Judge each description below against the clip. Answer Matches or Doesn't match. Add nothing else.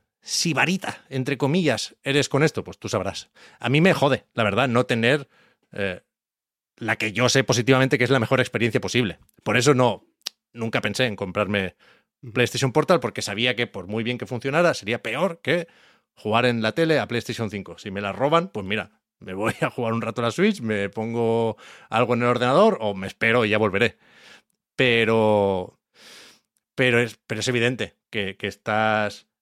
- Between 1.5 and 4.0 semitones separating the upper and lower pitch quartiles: Matches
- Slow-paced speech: Doesn't match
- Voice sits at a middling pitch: Doesn't match